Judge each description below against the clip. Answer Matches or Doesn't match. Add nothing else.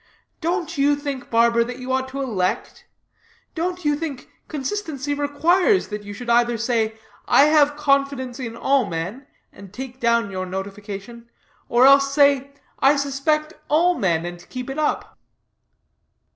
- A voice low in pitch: Doesn't match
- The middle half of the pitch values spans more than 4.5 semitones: Doesn't match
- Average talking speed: Matches